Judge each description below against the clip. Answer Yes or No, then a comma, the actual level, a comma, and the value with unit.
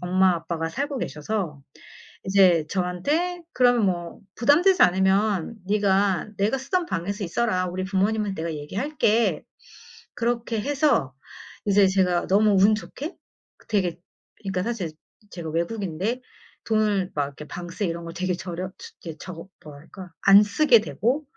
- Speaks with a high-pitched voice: Yes, high, 195 Hz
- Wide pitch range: No, average, 4.2 semitones